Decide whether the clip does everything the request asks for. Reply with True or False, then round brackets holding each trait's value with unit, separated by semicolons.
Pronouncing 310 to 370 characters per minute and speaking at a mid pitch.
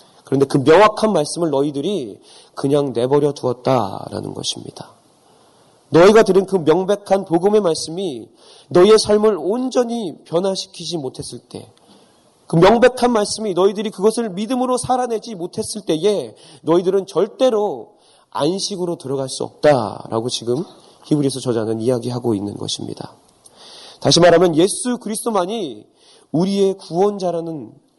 True (315 characters per minute; 180 Hz)